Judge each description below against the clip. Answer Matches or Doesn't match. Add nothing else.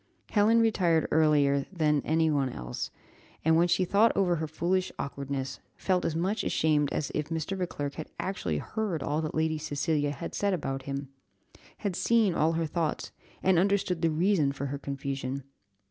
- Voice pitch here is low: Doesn't match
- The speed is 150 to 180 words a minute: Matches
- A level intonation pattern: Doesn't match